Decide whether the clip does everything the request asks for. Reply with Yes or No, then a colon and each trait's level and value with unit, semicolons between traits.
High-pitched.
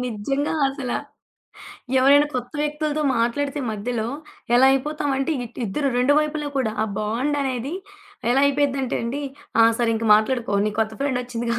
Yes: very high, 260 Hz